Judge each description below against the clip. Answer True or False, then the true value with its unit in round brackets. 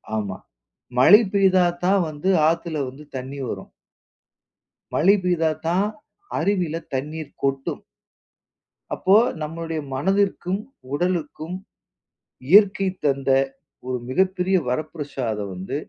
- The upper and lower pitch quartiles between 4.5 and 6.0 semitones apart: True (5.2 semitones)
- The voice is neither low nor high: True (165 Hz)